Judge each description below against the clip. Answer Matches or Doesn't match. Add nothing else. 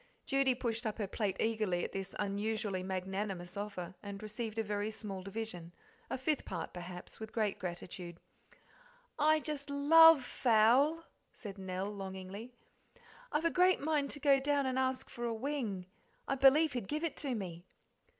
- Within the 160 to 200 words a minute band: Matches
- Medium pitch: Doesn't match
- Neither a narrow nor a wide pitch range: Doesn't match